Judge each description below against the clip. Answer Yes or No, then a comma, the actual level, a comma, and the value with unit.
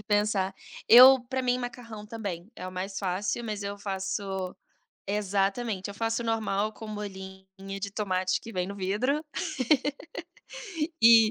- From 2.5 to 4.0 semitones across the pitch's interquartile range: Yes, average, 2.8 semitones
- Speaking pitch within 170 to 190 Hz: No, high, 205 Hz